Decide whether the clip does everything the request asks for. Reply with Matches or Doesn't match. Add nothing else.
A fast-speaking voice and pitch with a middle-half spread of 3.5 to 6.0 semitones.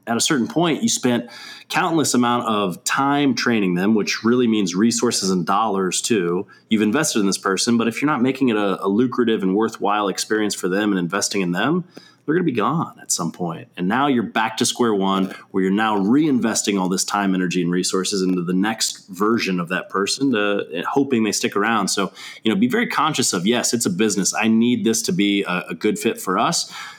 Matches